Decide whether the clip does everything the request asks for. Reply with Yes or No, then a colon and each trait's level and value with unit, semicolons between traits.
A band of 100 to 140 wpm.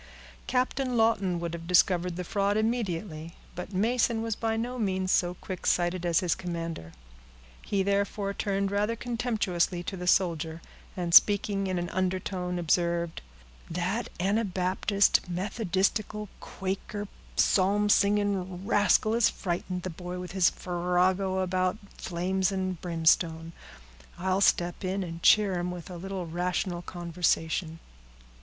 Yes: slow, 135 wpm